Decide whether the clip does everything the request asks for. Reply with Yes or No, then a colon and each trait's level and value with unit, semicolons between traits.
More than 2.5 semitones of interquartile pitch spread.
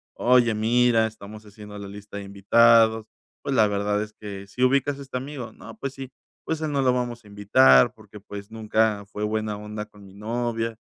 Yes: average, 2.9 semitones